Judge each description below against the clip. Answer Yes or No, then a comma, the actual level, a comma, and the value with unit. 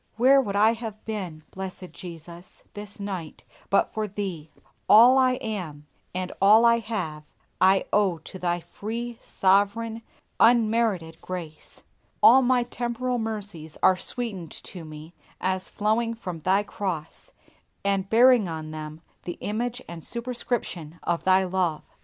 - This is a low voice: No, high, 200 Hz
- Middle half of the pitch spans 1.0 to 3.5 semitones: No, average, 4.7 semitones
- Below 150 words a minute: Yes, average, 140 wpm